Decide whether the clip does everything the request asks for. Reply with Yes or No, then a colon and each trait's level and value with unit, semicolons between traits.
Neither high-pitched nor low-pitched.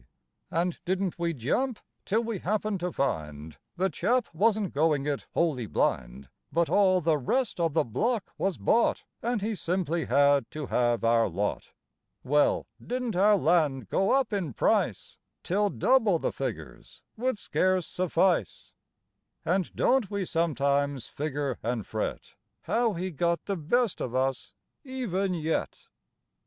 Yes: medium, 170 Hz